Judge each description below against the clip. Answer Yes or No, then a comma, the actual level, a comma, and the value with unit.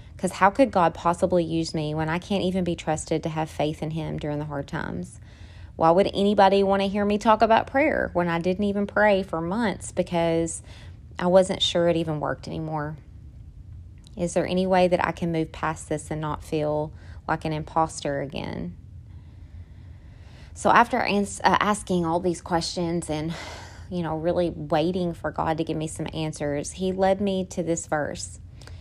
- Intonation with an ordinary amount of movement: Yes, average, 3.7 semitones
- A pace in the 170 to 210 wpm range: Yes, average, 185 wpm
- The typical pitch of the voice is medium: Yes, medium, 165 Hz